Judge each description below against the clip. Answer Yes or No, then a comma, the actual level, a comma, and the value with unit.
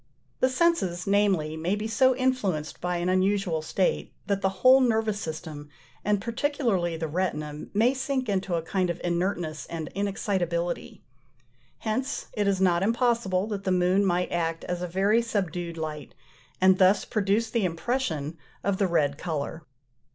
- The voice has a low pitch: No, high, 190 Hz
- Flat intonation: No, average, 4.0 semitones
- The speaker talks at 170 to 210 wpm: No, average, 160 wpm